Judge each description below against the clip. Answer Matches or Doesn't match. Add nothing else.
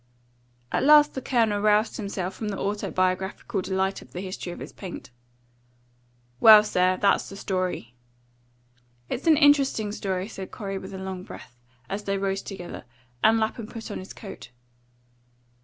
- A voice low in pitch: Doesn't match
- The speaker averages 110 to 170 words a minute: Matches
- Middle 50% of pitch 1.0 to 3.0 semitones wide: Matches